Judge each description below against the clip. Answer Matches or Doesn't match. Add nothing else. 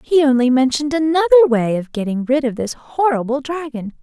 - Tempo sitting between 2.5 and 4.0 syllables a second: Doesn't match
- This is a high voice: Matches